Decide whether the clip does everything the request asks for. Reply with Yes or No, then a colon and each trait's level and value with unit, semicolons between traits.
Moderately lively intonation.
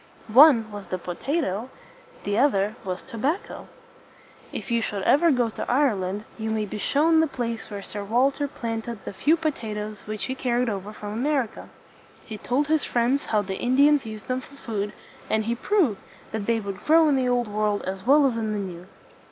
Yes: average, 4.7 semitones